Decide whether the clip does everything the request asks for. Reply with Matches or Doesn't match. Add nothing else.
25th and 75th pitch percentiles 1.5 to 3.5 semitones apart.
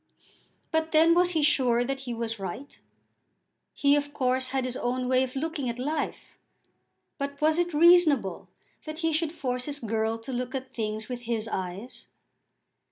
Doesn't match